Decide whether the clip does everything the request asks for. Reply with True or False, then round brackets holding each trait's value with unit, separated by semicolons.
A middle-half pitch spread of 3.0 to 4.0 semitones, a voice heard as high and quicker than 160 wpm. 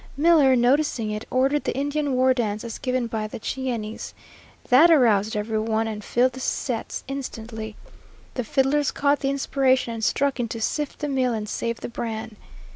True (3.6 semitones; 250 Hz; 175 wpm)